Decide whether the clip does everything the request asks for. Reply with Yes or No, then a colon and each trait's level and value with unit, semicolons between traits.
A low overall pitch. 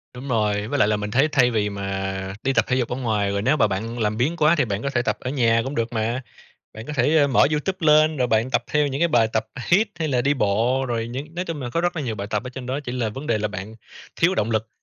Yes: low, 125 Hz